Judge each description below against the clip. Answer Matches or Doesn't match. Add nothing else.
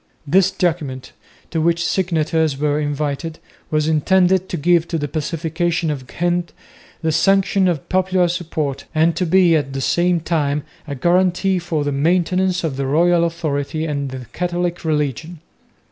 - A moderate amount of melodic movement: Matches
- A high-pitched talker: Doesn't match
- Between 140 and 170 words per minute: Matches